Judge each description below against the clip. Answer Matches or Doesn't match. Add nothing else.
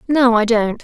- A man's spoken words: Doesn't match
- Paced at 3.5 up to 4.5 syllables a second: Matches